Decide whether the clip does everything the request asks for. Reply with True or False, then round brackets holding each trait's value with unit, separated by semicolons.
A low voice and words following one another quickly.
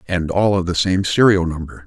True (90 Hz; 225 wpm)